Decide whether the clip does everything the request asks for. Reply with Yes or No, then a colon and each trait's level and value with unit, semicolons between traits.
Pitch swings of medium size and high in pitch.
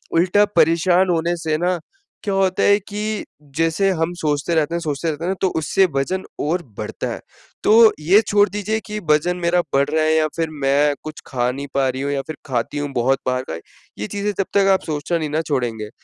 No: average, 4.6 semitones; medium, 165 Hz